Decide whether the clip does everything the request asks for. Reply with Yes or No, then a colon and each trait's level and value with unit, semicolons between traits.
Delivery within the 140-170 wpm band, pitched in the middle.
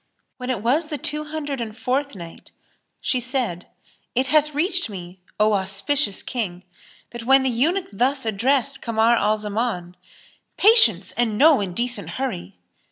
No: average, 150 wpm; high, 240 Hz